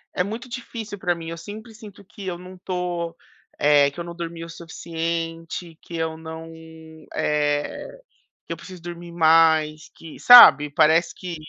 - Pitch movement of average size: No, narrow, 2.2 semitones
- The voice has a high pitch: No, medium, 170 Hz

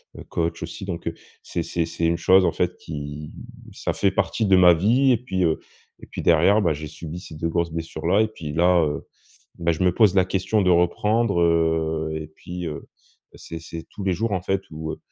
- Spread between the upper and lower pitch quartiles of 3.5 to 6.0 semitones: No, average, 2.8 semitones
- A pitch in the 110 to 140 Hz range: No, very low, 85 Hz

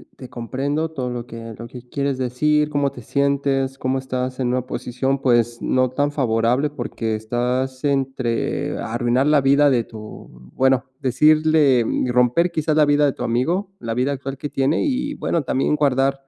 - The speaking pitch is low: Yes, low, 130 Hz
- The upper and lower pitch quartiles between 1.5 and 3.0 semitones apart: Yes, narrow, 2.6 semitones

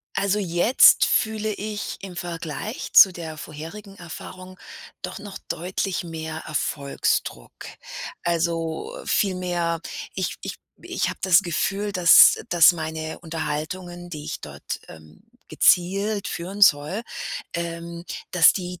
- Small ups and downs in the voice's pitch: No, average, 3.3 semitones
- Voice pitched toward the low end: No, medium, 175 Hz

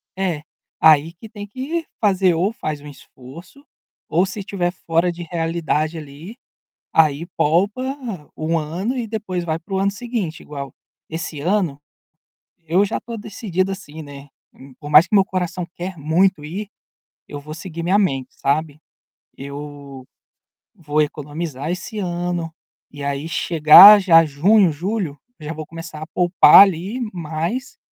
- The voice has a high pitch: No, medium, 170 Hz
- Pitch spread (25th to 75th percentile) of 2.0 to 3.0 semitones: No, average, 4.2 semitones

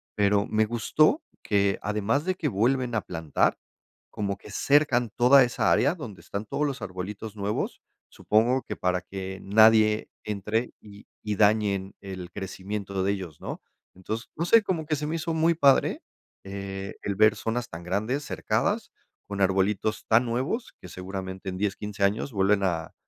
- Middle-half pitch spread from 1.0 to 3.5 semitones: No, average, 4.1 semitones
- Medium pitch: No, low, 105 Hz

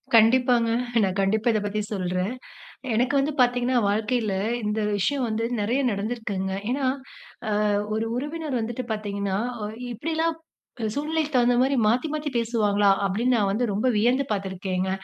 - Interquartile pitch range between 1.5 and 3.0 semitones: No, average, 3.7 semitones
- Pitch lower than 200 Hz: No, high, 225 Hz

